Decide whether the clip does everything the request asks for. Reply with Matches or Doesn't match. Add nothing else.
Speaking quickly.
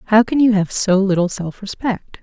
Matches